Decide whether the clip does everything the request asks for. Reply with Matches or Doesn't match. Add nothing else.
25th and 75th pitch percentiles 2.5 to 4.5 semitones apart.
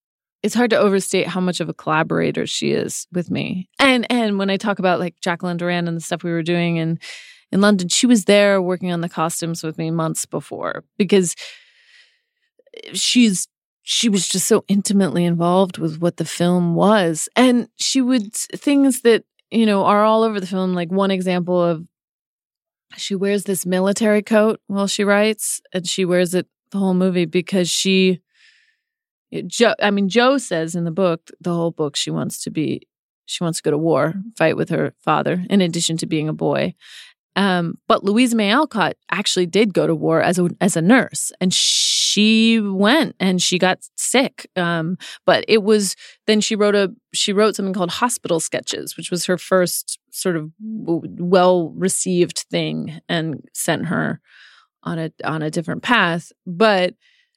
Matches